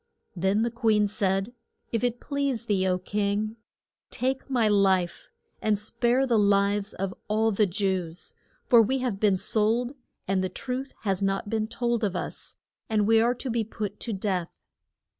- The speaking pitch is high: Yes, high, 210 Hz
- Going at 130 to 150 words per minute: No, average, 170 wpm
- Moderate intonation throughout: Yes, average, 3.3 semitones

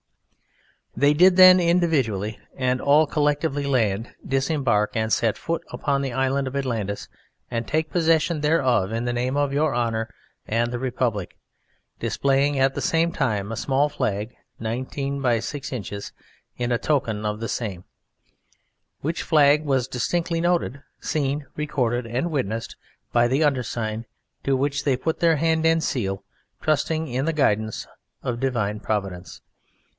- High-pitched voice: No, low, 135 Hz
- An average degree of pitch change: Yes, average, 4.6 semitones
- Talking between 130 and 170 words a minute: Yes, average, 150 wpm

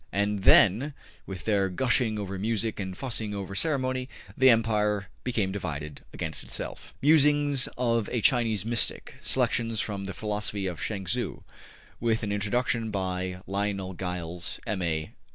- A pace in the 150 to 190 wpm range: No, average, 140 wpm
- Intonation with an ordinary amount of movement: Yes, average, 3.5 semitones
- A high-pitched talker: No, low, 105 Hz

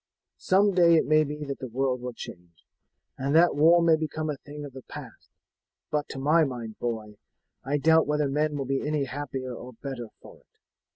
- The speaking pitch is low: No, medium, 145 Hz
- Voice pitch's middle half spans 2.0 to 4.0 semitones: Yes, average, 3.1 semitones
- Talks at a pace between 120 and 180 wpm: No, fast, 205 wpm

